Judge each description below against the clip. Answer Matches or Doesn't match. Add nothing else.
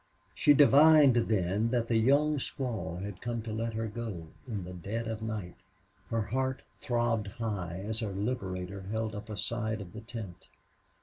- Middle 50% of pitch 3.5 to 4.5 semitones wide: Doesn't match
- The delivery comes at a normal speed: Matches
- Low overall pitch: Matches